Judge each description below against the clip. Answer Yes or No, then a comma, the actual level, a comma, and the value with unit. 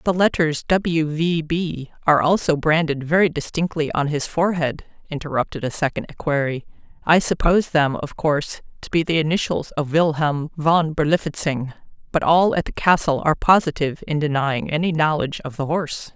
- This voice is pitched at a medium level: Yes, medium, 155 Hz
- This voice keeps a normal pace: Yes, average, 160 wpm